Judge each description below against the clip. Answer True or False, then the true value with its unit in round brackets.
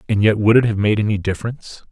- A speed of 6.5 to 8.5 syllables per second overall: True (7.1 syllables/s)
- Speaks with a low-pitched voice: True (105 Hz)